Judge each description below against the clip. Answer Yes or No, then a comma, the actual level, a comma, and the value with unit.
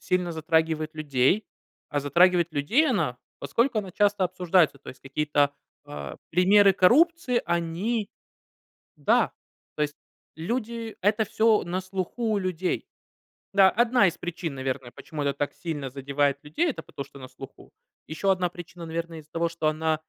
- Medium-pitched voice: Yes, medium, 170 Hz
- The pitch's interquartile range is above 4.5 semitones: Yes, average, 5.2 semitones